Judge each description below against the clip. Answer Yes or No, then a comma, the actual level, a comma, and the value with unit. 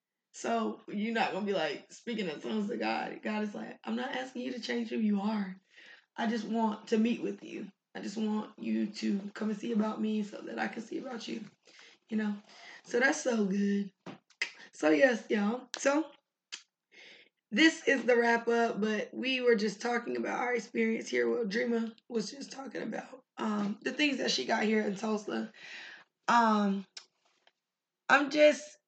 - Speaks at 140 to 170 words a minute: No, average, 185 wpm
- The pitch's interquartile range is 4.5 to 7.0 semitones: No, average, 3.0 semitones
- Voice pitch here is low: No, high, 225 Hz